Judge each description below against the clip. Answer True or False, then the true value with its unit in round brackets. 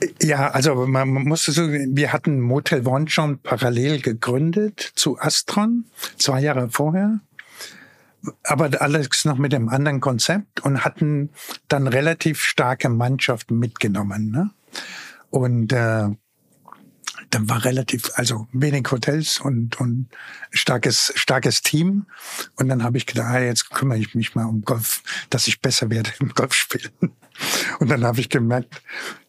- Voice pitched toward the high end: False (135 Hz)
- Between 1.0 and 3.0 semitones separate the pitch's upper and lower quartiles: False (3.8 semitones)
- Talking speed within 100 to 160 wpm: True (140 wpm)